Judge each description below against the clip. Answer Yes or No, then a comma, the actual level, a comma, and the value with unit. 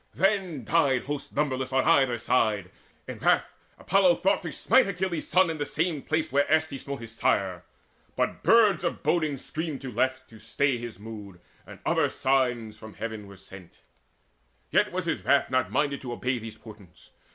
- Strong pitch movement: Yes, wide, 6.1 semitones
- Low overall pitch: Yes, low, 130 Hz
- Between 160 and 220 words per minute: Yes, average, 185 wpm